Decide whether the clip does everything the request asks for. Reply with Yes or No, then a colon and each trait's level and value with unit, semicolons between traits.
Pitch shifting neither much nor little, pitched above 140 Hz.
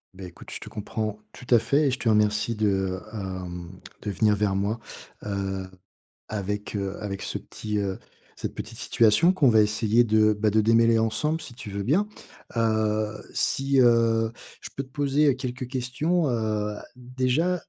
No: average, 3.5 semitones; low, 110 Hz